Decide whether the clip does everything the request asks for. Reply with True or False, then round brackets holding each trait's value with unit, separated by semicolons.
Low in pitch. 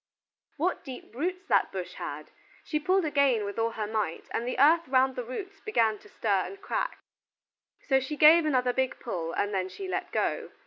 False (260 Hz)